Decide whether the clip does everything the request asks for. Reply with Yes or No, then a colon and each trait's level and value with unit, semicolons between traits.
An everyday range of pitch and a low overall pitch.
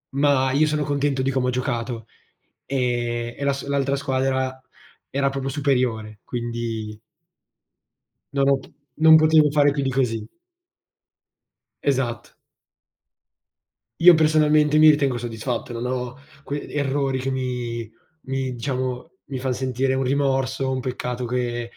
No: narrow, 2.3 semitones; low, 130 Hz